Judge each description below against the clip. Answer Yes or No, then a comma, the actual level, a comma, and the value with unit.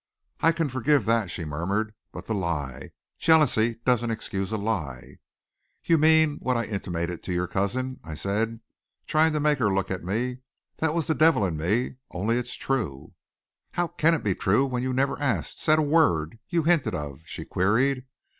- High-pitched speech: No, low, 115 Hz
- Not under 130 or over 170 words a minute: No, average, 185 wpm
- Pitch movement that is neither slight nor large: No, wide, 7.3 semitones